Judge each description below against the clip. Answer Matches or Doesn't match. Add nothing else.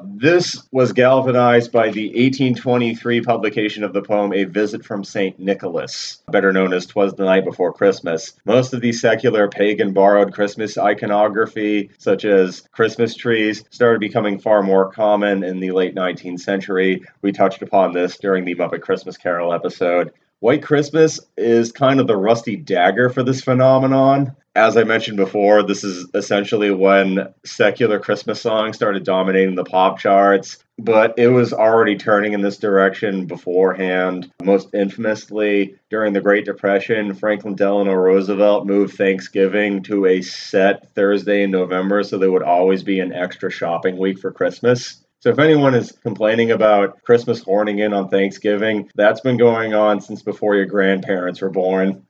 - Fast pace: Doesn't match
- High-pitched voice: Doesn't match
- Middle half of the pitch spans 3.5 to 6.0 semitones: Doesn't match